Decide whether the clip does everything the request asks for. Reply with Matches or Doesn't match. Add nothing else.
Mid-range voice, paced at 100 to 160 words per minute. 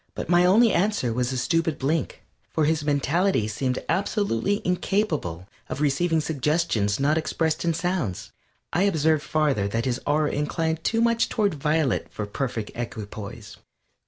Matches